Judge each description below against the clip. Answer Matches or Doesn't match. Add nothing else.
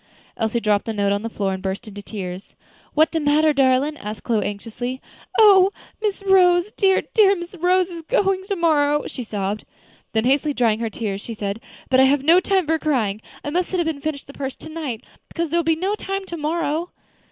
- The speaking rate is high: Matches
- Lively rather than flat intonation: Matches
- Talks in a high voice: Matches